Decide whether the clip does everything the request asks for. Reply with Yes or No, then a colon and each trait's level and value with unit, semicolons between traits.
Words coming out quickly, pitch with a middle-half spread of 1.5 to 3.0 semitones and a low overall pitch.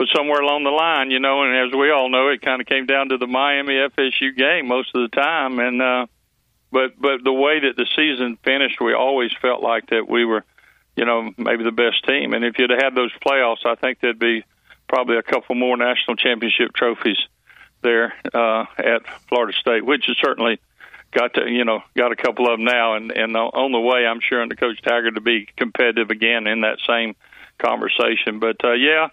Yes: fast, 220 wpm; narrow, 2.4 semitones; low, 125 Hz